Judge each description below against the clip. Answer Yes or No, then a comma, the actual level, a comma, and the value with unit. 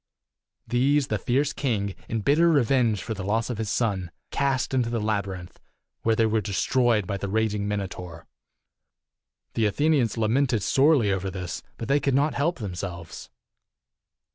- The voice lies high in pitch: No, low, 110 Hz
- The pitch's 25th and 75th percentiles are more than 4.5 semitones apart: Yes, average, 4.9 semitones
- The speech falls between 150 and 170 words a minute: Yes, average, 155 wpm